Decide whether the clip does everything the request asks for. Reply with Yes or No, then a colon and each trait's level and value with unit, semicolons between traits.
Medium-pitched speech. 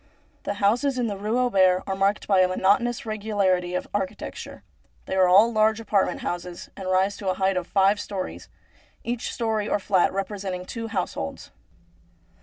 No: high, 200 Hz